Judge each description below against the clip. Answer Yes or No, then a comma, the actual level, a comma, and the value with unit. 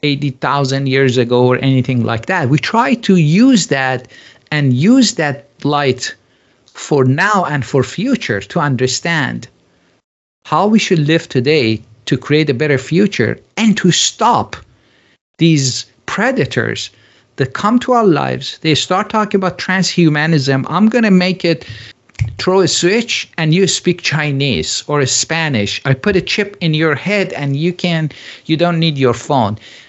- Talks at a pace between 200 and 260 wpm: No, average, 155 wpm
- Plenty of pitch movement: Yes, wide, 5.9 semitones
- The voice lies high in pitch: No, medium, 150 Hz